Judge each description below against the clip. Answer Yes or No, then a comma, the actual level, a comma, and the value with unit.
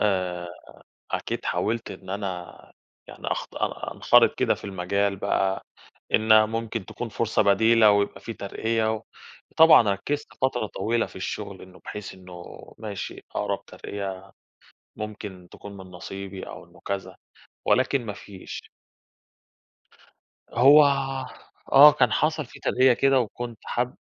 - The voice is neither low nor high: No, low, 105 Hz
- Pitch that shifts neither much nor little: Yes, average, 3.2 semitones